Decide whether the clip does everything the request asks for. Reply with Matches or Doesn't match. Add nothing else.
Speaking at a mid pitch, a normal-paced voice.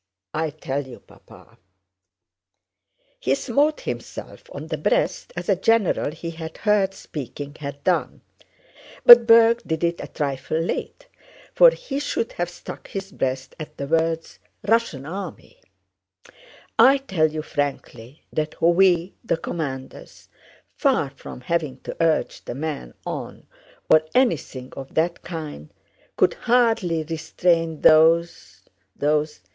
Doesn't match